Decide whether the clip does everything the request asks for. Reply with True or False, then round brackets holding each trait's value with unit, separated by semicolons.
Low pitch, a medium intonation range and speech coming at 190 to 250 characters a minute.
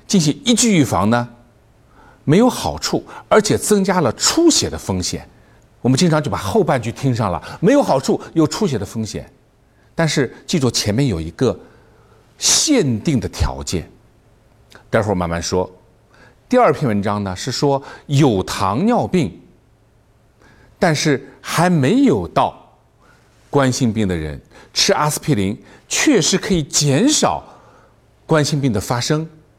False (130 Hz; 6.2 semitones; 210 characters per minute)